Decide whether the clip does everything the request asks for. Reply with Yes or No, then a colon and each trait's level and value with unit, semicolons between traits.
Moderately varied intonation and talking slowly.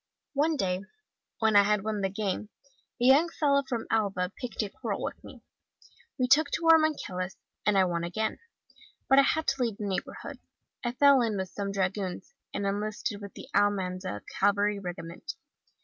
No: average, 4.9 semitones; average, 180 wpm